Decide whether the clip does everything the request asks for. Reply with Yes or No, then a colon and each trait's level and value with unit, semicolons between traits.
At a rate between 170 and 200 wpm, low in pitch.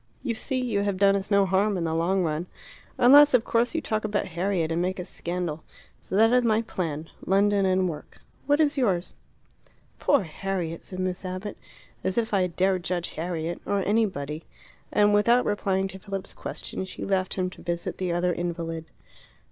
No: average, 190 wpm; high, 190 Hz